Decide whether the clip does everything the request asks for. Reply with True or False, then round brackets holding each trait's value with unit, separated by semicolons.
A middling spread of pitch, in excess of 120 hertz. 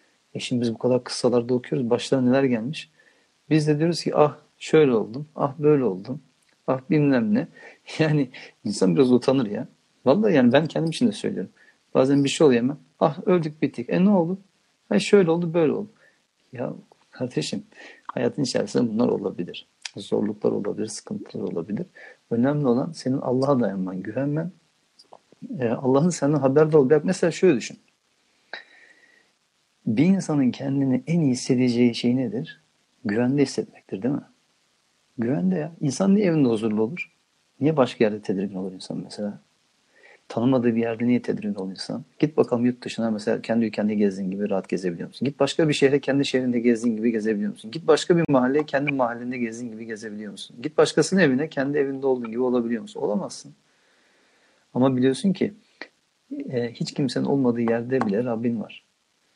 True (4.8 semitones; 135 Hz)